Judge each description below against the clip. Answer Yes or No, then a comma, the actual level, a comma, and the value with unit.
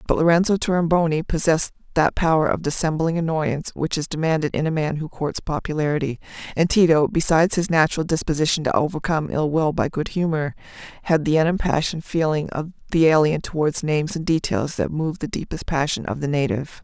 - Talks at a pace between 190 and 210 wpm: No, average, 180 wpm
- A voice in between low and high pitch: Yes, medium, 160 Hz